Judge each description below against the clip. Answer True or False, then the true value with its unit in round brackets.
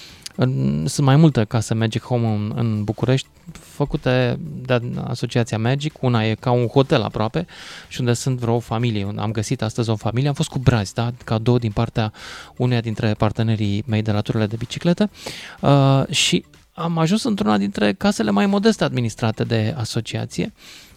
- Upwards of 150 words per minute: True (165 wpm)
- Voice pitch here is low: True (120 Hz)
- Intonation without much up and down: False (3.8 semitones)